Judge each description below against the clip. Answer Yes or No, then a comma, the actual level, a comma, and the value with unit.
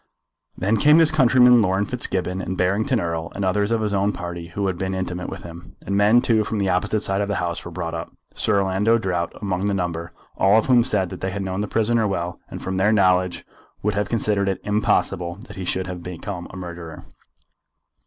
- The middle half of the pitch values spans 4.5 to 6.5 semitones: No, average, 2.7 semitones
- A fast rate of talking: Yes, fast, 225 wpm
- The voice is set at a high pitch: No, very low, 95 Hz